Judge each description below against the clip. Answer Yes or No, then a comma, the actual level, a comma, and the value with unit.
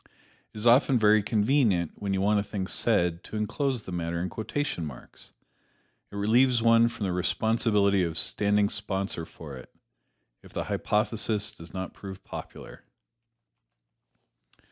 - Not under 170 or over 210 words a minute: No, average, 145 wpm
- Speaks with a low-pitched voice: Yes, low, 105 Hz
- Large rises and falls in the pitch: No, average, 3.4 semitones